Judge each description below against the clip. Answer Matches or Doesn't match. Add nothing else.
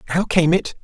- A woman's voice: Doesn't match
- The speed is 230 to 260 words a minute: Doesn't match